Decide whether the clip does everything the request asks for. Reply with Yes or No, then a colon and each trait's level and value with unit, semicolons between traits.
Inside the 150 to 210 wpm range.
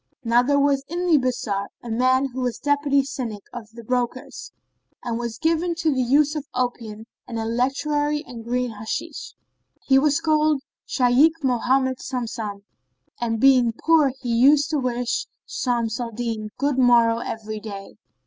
Yes: average, 160 wpm